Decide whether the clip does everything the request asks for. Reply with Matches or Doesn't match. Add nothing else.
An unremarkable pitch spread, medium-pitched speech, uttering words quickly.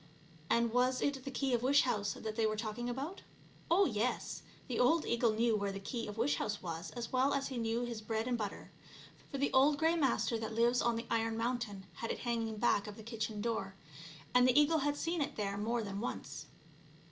Doesn't match